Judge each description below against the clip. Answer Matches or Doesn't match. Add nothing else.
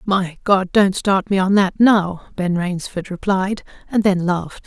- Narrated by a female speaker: Matches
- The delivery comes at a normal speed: Matches